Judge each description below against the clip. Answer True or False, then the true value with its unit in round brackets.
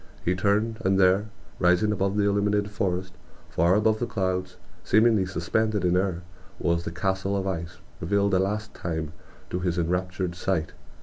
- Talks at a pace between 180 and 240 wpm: False (170 wpm)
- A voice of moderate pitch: False (95 Hz)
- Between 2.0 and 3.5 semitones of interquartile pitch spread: True (2.4 semitones)